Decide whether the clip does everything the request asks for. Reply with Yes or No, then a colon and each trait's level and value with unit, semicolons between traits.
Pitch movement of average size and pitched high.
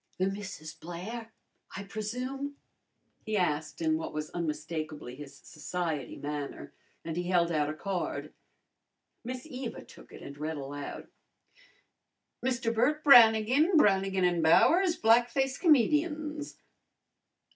No: wide, 8.1 semitones; high, 195 Hz